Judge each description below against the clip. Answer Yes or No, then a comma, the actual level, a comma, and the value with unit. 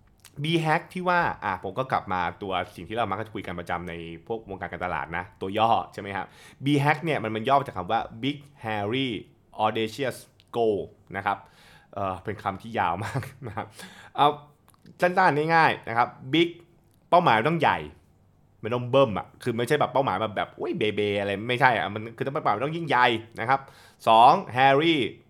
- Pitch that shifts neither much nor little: No, wide, 5.9 semitones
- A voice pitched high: No, low, 115 Hz